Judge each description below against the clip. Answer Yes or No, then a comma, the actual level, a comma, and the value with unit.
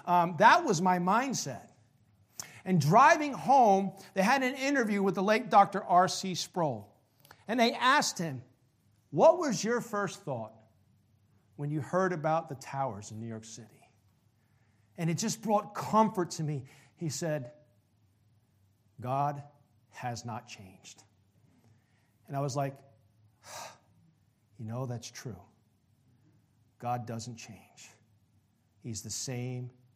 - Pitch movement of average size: No, wide, 8.1 semitones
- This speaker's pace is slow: Yes, slow, 130 wpm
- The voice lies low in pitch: Yes, low, 125 Hz